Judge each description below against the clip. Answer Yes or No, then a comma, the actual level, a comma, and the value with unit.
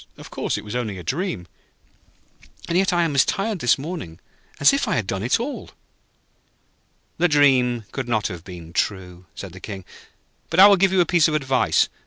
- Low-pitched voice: Yes, low, 130 Hz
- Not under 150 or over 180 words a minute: No, fast, 205 wpm